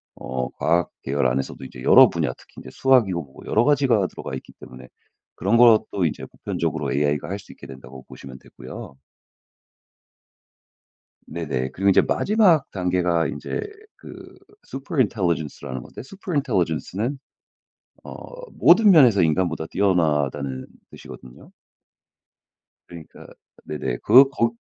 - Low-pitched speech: Yes, very low, 90 Hz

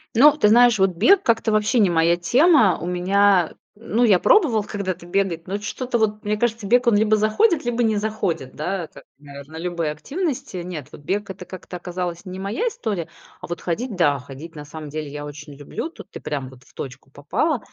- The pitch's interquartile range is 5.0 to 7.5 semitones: Yes, wide, 5.5 semitones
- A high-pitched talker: Yes, high, 195 Hz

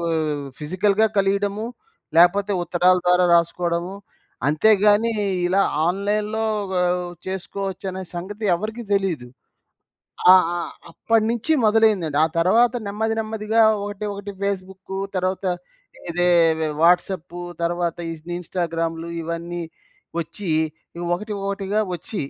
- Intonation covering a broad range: No, average, 3.2 semitones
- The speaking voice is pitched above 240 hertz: No, high, 190 Hz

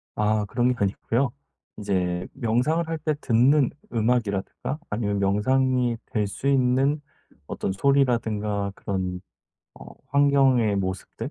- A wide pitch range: No, average, 4.8 semitones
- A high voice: No, low, 115 Hz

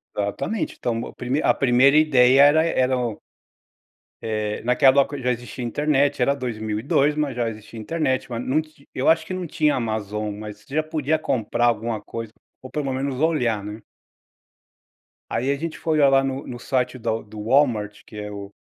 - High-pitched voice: No, low, 125 Hz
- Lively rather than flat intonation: No, average, 4.3 semitones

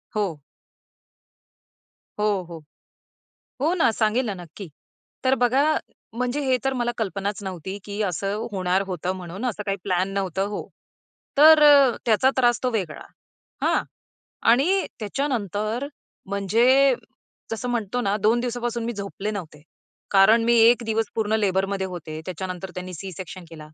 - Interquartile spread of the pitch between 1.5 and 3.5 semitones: No, average, 4.2 semitones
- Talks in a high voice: Yes, high, 210 Hz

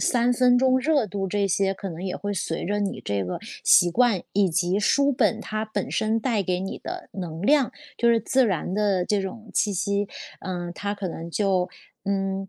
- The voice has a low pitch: No, high, 200 Hz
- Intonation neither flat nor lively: Yes, average, 3.4 semitones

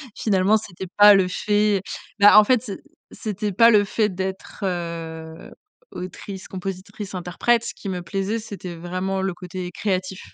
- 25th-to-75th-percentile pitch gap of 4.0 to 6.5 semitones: No, narrow, 2.4 semitones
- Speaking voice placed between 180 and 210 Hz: Yes, high, 190 Hz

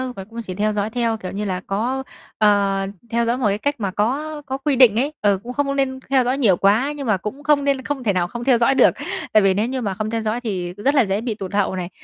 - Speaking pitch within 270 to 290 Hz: No, high, 225 Hz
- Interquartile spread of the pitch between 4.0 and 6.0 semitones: Yes, average, 4.7 semitones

